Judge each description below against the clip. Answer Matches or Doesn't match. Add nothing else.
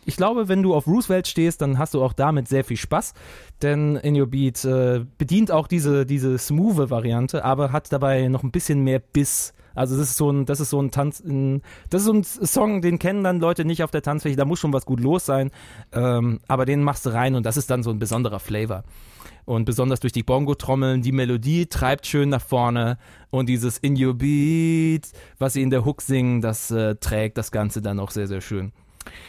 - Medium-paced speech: Doesn't match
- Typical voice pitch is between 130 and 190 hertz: Matches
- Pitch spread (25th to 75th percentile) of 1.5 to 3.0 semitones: Doesn't match